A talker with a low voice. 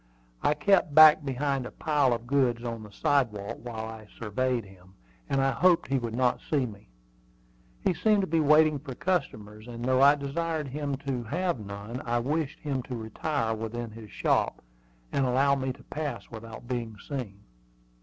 Yes: low, 130 Hz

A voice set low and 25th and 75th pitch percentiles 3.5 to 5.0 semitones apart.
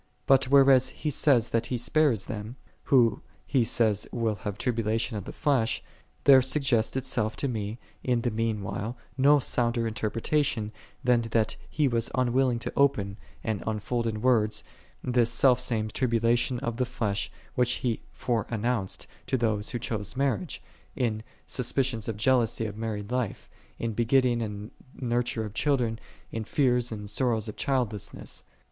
No: low, 115 Hz; average, 2.7 semitones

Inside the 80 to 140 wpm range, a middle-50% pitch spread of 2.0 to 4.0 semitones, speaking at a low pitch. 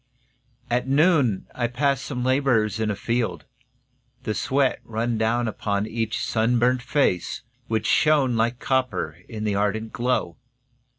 Yes: slow, 135 wpm; average, 2.8 semitones; low, 120 Hz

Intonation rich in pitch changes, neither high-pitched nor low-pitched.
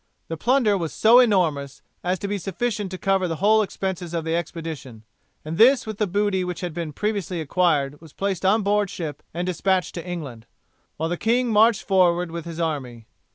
No: average, 3.9 semitones; medium, 180 Hz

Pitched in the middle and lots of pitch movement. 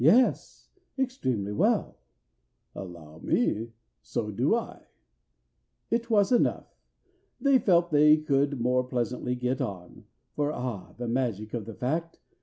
No: low, 125 Hz; wide, 6.5 semitones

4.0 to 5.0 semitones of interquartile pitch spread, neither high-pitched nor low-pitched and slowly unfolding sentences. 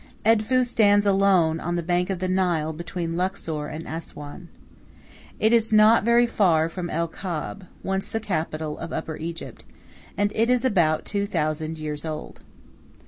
No: average, 4.3 semitones; medium, 180 Hz; average, 160 wpm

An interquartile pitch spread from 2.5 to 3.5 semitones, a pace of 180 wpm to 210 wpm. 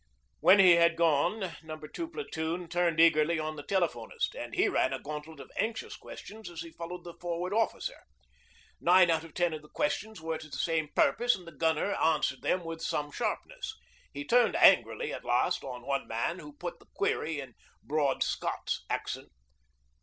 Yes: average, 3.2 semitones; average, 185 wpm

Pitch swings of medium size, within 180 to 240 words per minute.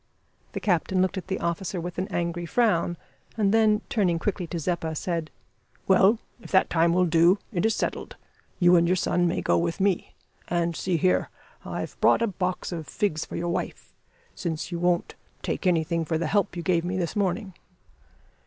No: narrow, 2.0 semitones; average, 190 wpm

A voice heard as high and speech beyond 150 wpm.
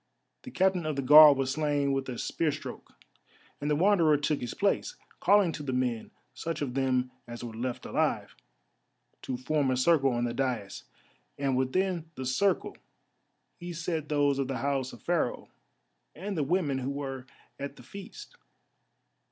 No: medium, 140 Hz; average, 170 wpm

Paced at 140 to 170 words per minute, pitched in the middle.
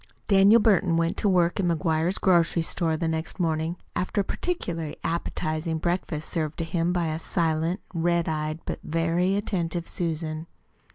Yes: average, 160 wpm; medium, 170 Hz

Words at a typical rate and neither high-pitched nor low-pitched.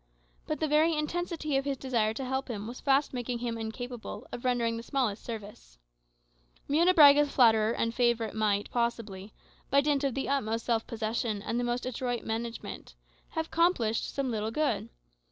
No: average, 170 wpm; high, 240 Hz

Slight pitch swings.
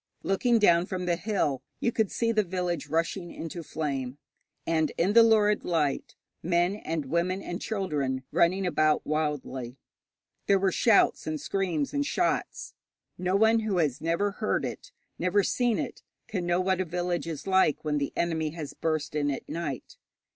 No: average, 4.2 semitones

